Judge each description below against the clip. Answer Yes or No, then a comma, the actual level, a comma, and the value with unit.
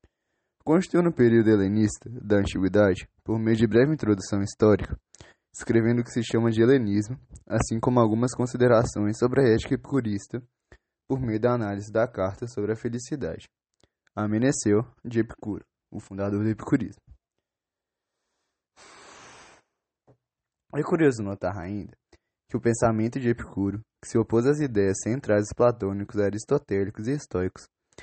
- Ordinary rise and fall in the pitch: Yes, average, 3.0 semitones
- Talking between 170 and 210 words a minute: No, slow, 135 wpm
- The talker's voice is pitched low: Yes, low, 115 Hz